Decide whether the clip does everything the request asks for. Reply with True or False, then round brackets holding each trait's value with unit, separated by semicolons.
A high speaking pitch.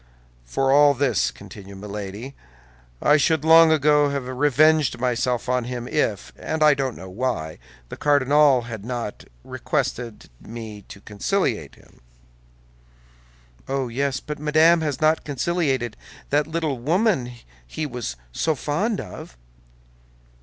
False (135 Hz)